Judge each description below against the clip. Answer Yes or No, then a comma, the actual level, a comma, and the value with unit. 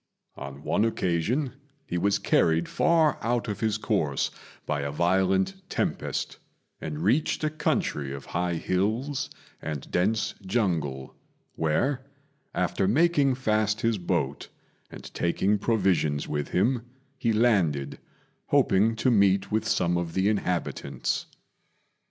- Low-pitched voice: Yes, very low, 95 Hz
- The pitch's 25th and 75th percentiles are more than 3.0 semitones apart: Yes, average, 5.2 semitones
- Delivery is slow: Yes, slow, 125 wpm